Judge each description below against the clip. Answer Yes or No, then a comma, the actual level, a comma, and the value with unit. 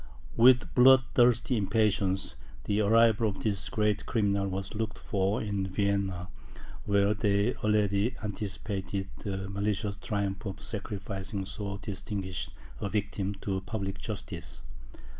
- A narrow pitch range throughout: Yes, narrow, 1.7 semitones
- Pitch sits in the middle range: No, low, 100 Hz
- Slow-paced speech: Yes, slow, 120 wpm